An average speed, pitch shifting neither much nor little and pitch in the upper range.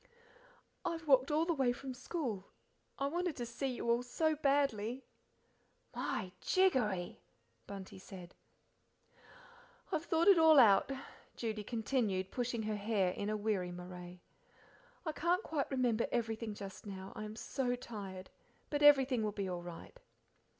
No: average, 150 wpm; wide, 5.8 semitones; high, 235 Hz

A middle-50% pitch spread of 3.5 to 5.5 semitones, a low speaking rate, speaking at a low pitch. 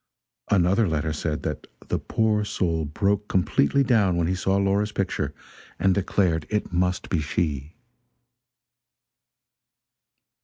Yes: average, 4.0 semitones; slow, 120 wpm; very low, 90 Hz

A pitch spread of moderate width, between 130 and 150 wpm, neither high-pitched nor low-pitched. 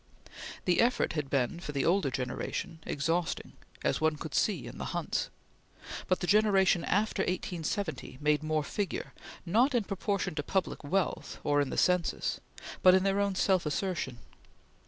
No: average, 4.6 semitones; average, 160 wpm; medium, 175 Hz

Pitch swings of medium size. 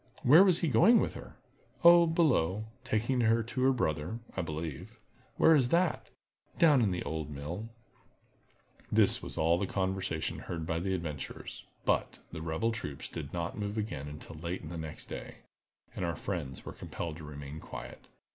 No: wide, 6.9 semitones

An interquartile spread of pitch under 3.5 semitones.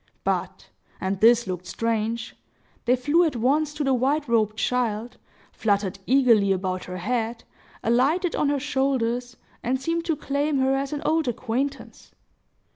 No: average, 4.1 semitones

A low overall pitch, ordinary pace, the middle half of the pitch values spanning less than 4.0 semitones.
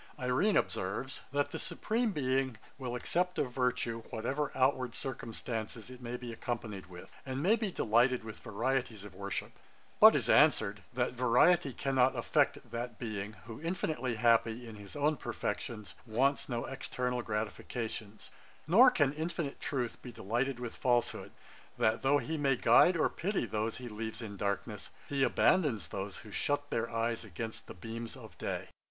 Yes: low, 125 Hz; average, 160 wpm; average, 3.5 semitones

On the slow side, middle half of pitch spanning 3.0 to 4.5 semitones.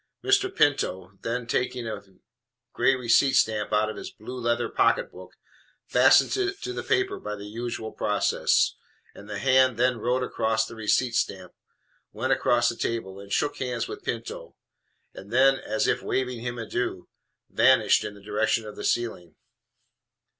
No: average, 170 wpm; average, 3.3 semitones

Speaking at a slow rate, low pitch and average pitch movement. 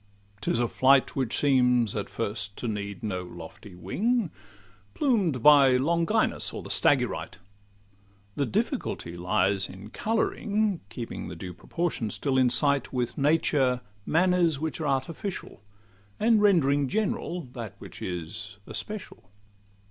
No: slow, 130 wpm; low, 130 Hz; wide, 7.8 semitones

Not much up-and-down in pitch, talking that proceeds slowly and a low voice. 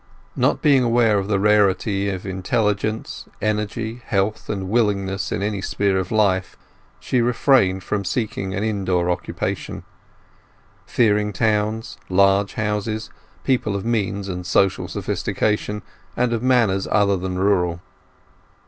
Yes: narrow, 2.3 semitones; slow, 130 wpm; low, 105 Hz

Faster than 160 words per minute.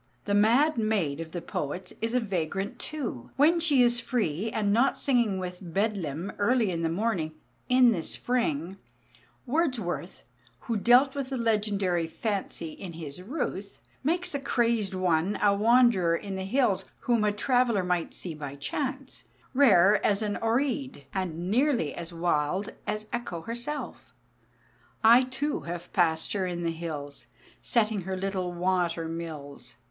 No: average, 150 wpm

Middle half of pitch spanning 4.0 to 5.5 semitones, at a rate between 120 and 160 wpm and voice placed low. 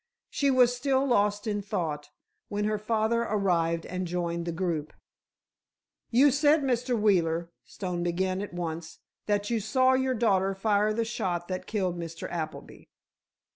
No: average, 5.1 semitones; average, 150 wpm; high, 200 Hz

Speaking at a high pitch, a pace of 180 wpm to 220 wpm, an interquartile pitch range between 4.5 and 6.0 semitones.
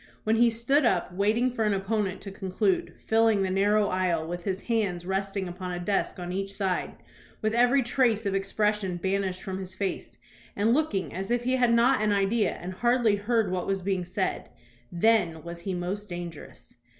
No: high, 195 Hz; average, 190 wpm; average, 3.3 semitones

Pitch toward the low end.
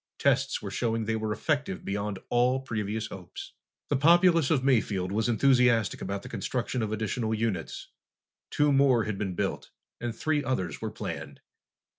Yes: low, 115 Hz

